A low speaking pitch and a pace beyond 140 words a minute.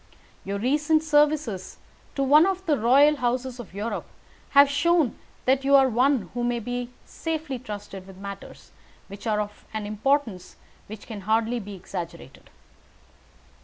No: high, 245 Hz; average, 150 wpm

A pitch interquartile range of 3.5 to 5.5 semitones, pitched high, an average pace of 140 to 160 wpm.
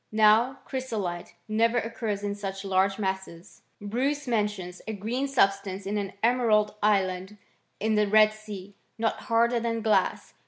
No: average, 2.7 semitones; high, 210 Hz; average, 145 wpm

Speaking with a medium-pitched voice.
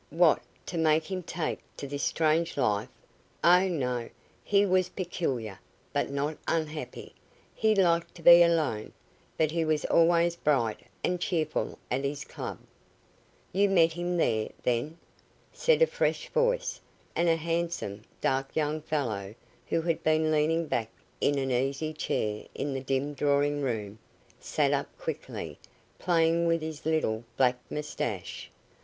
Yes: medium, 155 Hz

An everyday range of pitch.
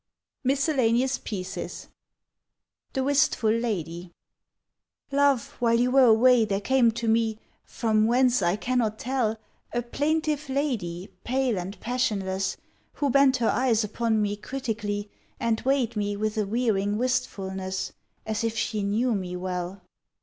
Yes: average, 3.9 semitones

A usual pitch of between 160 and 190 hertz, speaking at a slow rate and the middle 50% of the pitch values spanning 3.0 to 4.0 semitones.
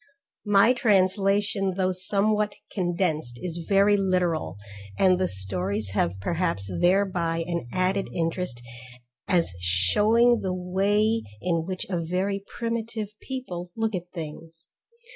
Yes: medium, 185 Hz; slow, 120 wpm; average, 3.5 semitones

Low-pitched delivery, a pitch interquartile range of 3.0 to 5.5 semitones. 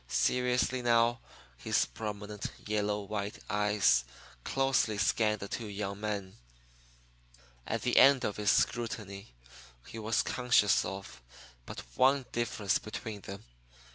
No: low, 105 Hz; narrow, 2.6 semitones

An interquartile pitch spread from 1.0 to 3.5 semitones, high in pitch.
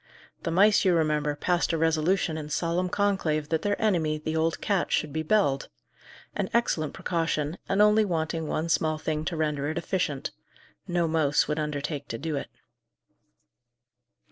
No: average, 2.8 semitones; medium, 160 Hz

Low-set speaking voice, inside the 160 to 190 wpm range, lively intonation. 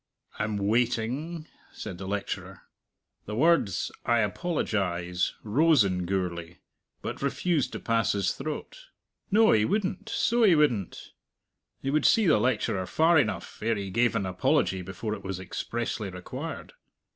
No: low, 110 Hz; average, 145 wpm; wide, 7.9 semitones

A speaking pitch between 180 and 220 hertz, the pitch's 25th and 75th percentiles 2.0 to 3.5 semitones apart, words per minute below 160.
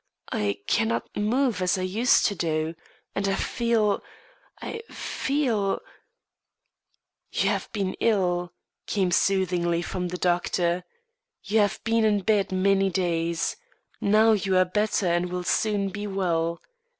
Yes: high, 190 Hz; average, 3.0 semitones; average, 140 wpm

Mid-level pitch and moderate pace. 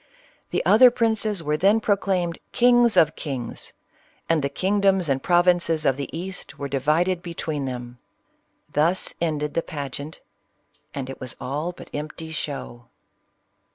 Yes: medium, 160 Hz; average, 155 wpm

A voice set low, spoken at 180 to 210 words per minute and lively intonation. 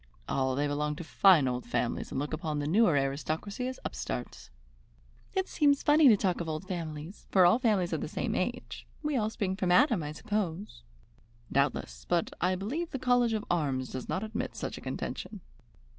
No: medium, 180 Hz; average, 190 wpm; wide, 6.6 semitones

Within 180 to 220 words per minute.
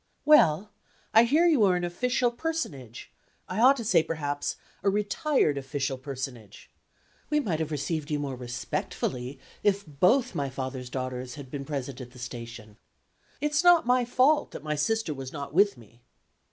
No: average, 165 wpm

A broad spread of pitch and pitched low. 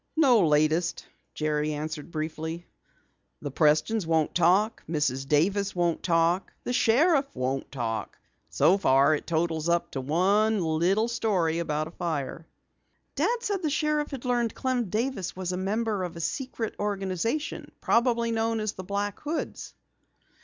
No: wide, 6.4 semitones; medium, 185 Hz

